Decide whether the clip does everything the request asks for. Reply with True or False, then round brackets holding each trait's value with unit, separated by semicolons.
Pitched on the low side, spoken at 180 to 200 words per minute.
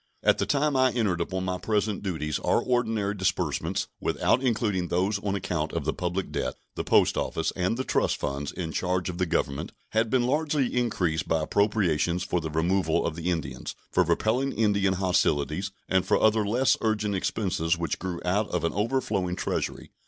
True (95 Hz; 185 wpm)